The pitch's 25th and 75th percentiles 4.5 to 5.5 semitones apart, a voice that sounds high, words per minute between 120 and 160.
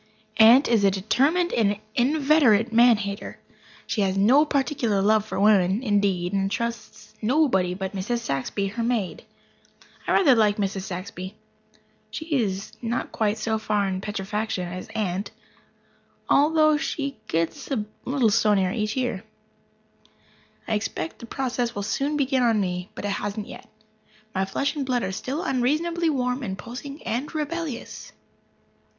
Yes: average, 5.0 semitones; high, 220 Hz; average, 150 wpm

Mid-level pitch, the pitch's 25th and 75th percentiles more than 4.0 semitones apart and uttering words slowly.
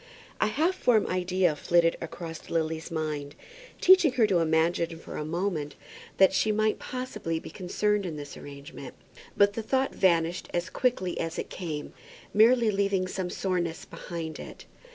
No: medium, 180 Hz; average, 4.4 semitones; average, 155 wpm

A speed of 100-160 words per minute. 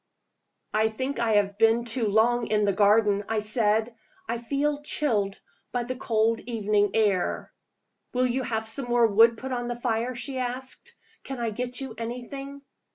No: average, 170 wpm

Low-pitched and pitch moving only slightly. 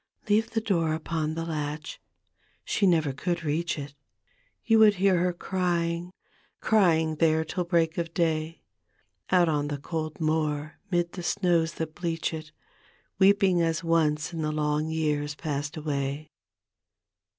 No: medium, 160 Hz; narrow, 2.3 semitones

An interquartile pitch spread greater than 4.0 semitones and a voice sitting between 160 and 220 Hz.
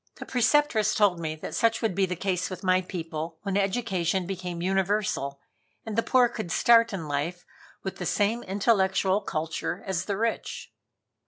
No: average, 3.4 semitones; high, 190 Hz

